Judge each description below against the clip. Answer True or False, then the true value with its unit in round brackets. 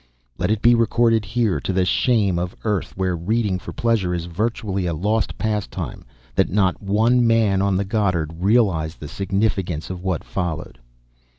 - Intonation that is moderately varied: True (3.7 semitones)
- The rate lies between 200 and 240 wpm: False (175 wpm)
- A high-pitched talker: False (100 Hz)